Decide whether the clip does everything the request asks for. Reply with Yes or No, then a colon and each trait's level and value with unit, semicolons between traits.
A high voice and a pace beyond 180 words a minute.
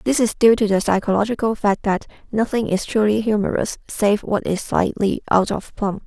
Yes: high, 210 Hz; average, 190 wpm